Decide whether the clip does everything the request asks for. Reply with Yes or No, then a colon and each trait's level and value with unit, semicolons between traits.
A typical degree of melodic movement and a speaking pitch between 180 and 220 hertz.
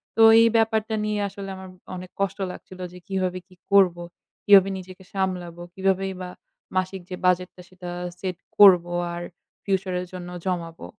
No: narrow, 1.3 semitones; medium, 185 Hz